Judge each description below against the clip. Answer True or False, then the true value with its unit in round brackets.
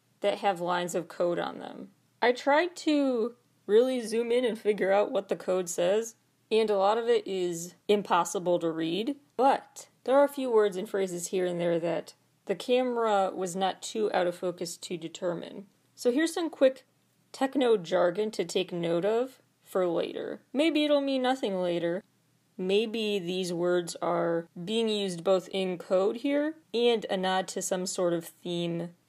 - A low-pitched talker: False (195 Hz)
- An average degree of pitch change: True (4.7 semitones)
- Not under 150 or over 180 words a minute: True (175 wpm)